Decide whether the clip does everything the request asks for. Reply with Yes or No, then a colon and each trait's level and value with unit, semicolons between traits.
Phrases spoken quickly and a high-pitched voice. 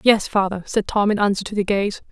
Yes: fast, 255 wpm; high, 200 Hz